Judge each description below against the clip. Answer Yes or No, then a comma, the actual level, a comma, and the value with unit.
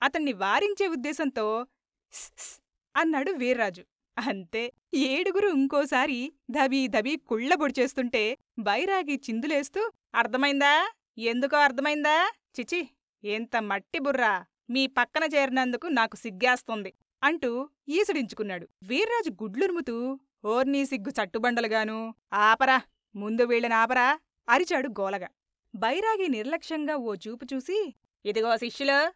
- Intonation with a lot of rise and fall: No, average, 4.7 semitones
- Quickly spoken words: No, average, 90 wpm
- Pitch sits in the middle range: No, very high, 265 Hz